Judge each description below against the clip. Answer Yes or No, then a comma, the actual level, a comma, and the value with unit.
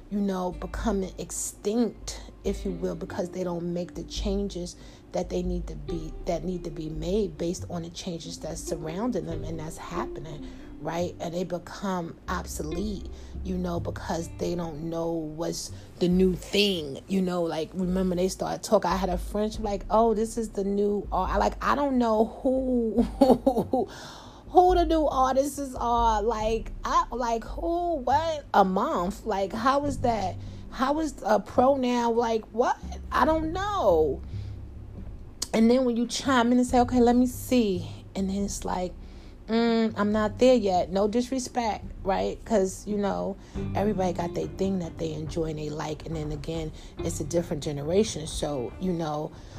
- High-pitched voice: Yes, high, 195 Hz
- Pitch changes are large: Yes, wide, 5.8 semitones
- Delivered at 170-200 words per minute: Yes, average, 175 wpm